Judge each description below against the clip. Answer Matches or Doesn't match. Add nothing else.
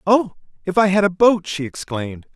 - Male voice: Matches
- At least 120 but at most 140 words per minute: Doesn't match